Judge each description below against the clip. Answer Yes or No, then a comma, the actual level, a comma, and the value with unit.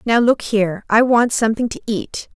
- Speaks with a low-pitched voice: No, high, 225 Hz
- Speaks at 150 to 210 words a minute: Yes, average, 200 wpm